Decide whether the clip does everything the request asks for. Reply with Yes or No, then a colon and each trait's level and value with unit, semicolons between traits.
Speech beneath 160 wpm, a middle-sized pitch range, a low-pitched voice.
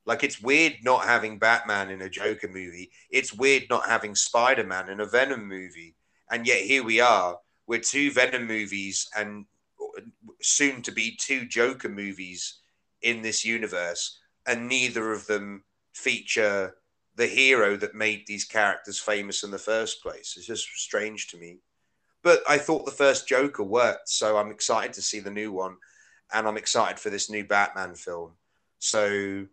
No: average, 170 wpm; average, 3.4 semitones; low, 105 Hz